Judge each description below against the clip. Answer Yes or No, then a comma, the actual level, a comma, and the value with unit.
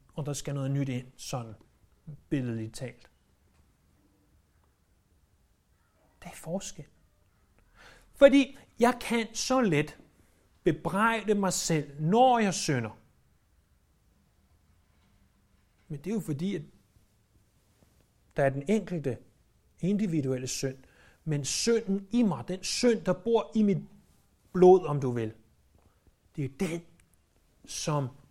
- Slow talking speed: Yes, slow, 110 wpm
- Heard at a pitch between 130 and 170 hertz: Yes, low, 135 Hz